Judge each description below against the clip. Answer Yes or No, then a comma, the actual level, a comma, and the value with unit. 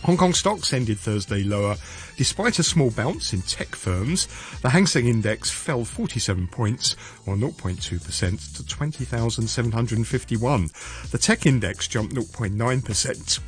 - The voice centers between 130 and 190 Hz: No, low, 115 Hz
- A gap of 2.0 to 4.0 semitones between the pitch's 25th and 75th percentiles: No, average, 4.6 semitones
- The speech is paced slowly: Yes, slow, 130 wpm